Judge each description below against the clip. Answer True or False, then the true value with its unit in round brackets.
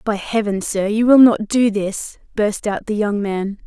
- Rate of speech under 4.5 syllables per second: True (4.2 syllables/s)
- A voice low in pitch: False (210 Hz)